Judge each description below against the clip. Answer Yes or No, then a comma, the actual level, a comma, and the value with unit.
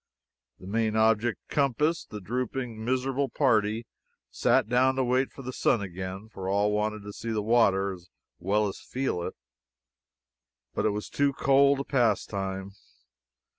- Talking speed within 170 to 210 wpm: No, average, 155 wpm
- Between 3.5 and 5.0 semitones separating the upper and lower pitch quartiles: Yes, average, 4.2 semitones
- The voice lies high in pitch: No, low, 110 Hz